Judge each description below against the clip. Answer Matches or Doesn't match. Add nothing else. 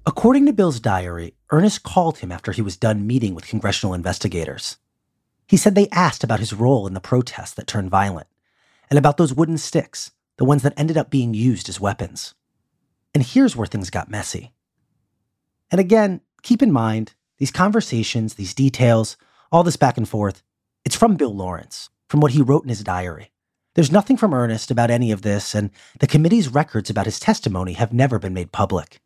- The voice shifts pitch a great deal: Matches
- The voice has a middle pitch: Doesn't match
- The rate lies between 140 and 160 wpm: Doesn't match